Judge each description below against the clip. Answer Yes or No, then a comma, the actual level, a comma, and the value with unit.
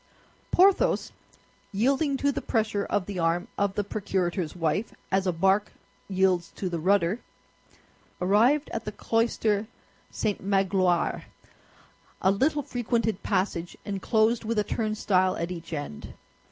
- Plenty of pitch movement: No, average, 3.4 semitones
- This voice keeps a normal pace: No, slow, 125 wpm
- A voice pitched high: Yes, high, 200 Hz